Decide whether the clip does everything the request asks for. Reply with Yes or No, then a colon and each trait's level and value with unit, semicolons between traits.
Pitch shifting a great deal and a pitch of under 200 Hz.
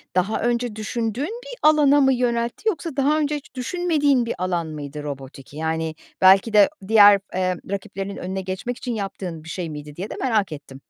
No: wide, 7.0 semitones; high, 205 Hz